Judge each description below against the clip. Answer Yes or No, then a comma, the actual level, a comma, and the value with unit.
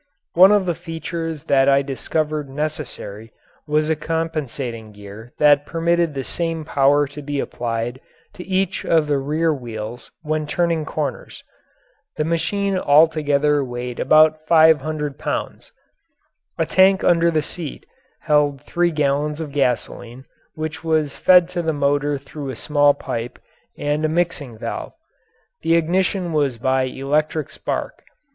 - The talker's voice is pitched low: No, medium, 150 Hz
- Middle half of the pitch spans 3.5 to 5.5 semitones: No, average, 3.0 semitones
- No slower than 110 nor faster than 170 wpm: Yes, average, 140 wpm